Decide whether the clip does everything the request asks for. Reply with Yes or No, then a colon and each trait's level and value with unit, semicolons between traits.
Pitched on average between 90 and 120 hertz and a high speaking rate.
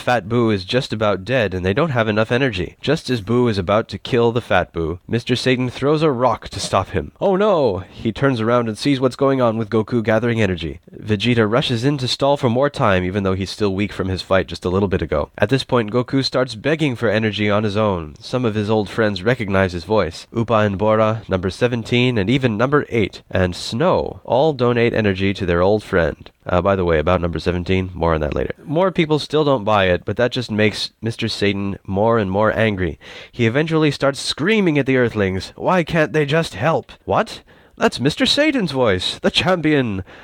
Yes: low, 115 Hz; fast, 220 wpm